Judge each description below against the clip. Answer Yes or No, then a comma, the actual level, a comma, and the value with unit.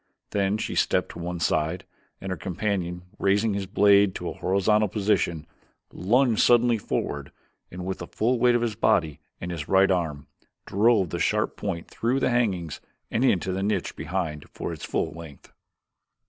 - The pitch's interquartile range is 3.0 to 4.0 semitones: Yes, average, 3.7 semitones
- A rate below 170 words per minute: No, average, 175 wpm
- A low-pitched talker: Yes, very low, 95 Hz